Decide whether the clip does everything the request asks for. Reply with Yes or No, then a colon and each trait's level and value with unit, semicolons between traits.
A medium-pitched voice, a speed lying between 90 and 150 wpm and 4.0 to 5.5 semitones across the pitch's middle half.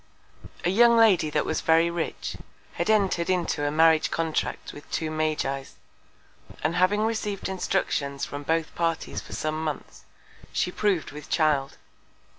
No: medium, 165 Hz; average, 145 wpm; average, 3.4 semitones